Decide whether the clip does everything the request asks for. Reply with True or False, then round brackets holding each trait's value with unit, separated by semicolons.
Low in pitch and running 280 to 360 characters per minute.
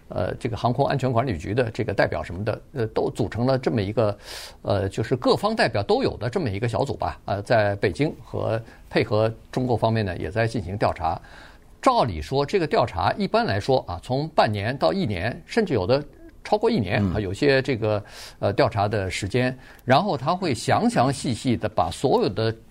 True (115 Hz; 300 characters per minute)